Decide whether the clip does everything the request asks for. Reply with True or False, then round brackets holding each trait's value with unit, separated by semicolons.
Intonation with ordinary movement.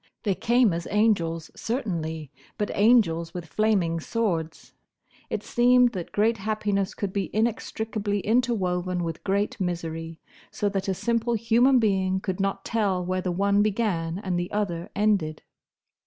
True (3.8 semitones)